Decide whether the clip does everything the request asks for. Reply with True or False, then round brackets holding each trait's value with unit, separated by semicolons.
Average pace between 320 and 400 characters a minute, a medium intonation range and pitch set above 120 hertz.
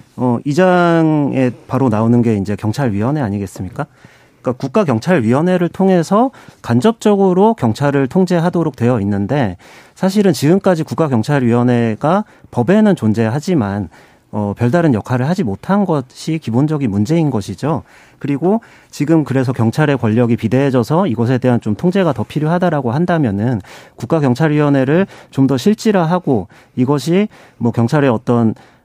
False (340 characters per minute; 6.6 semitones; 140 Hz)